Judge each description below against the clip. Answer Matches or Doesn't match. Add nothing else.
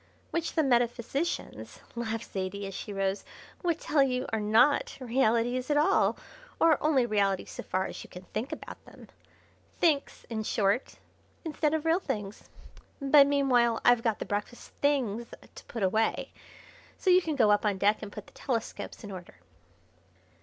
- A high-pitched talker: Matches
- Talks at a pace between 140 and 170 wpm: Matches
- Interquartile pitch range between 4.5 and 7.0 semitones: Matches